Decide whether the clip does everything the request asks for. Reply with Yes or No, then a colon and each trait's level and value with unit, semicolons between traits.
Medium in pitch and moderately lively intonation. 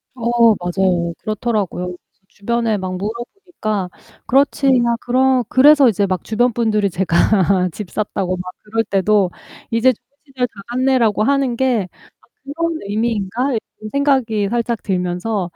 No: high, 220 Hz; average, 4.0 semitones